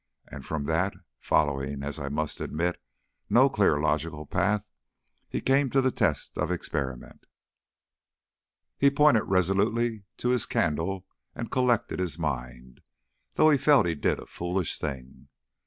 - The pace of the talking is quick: No, average, 140 wpm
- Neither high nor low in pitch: No, very low, 85 Hz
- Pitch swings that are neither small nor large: No, wide, 7.8 semitones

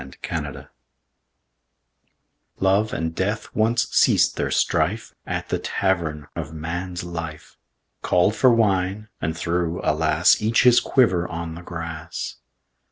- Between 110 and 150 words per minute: Yes, slow, 135 wpm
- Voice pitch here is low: Yes, very low, 90 Hz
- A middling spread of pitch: Yes, average, 4.0 semitones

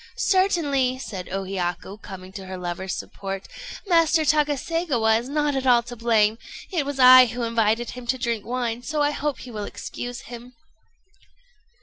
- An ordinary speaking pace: Yes, average, 165 wpm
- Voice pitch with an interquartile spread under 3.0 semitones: No, average, 5.1 semitones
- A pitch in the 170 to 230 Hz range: No, high, 245 Hz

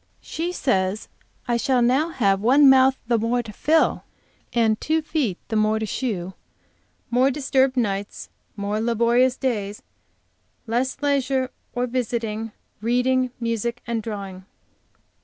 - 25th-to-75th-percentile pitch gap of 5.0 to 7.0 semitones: No, average, 3.2 semitones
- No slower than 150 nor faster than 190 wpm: No, slow, 135 wpm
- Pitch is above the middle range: Yes, high, 235 Hz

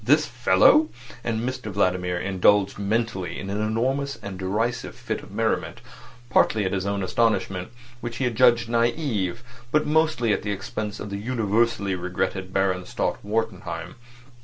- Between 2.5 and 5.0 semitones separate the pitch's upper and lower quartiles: Yes, average, 3.8 semitones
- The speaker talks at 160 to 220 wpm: No, average, 150 wpm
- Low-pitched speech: Yes, low, 105 Hz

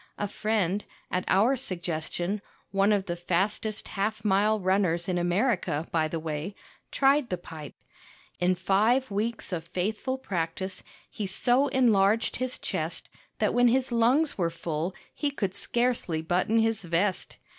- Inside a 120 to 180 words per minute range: Yes, average, 145 wpm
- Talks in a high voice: Yes, high, 195 Hz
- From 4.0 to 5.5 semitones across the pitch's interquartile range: Yes, average, 4.5 semitones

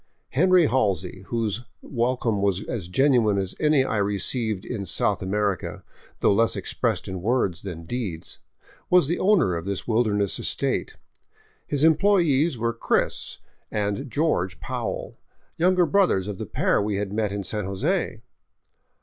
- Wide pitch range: Yes, wide, 6.0 semitones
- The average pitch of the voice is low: Yes, low, 110 Hz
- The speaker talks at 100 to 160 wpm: Yes, average, 150 wpm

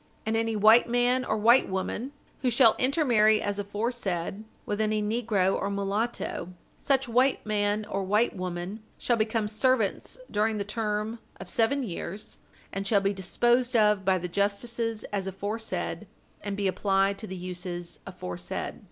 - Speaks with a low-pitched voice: No, high, 210 Hz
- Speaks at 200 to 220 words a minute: No, average, 155 wpm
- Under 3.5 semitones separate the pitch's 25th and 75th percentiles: Yes, average, 2.8 semitones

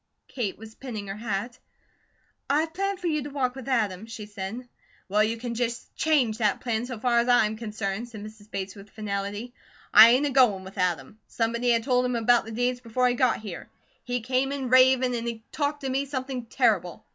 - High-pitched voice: Yes, high, 235 Hz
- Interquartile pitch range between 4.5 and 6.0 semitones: No, average, 3.1 semitones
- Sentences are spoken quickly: Yes, fast, 215 wpm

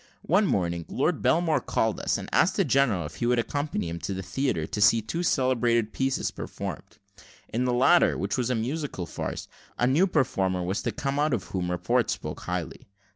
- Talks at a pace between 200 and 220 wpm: Yes, fast, 205 wpm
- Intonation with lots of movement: Yes, wide, 6.9 semitones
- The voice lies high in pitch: No, low, 120 Hz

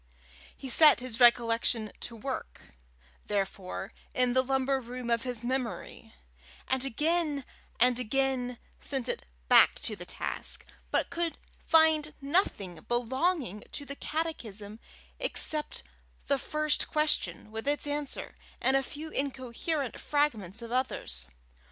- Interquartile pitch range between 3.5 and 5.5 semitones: Yes, average, 4.0 semitones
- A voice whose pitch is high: Yes, very high, 260 Hz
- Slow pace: Yes, slow, 125 wpm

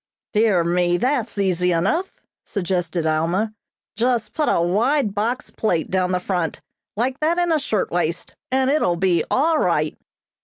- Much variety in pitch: Yes, wide, 6.5 semitones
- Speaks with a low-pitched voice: No, high, 200 Hz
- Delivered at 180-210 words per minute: No, average, 155 wpm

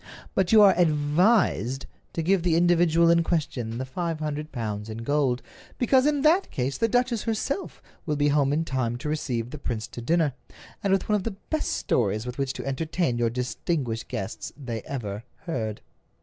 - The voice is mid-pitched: Yes, medium, 150 Hz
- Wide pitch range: Yes, wide, 6.3 semitones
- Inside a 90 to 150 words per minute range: No, average, 190 wpm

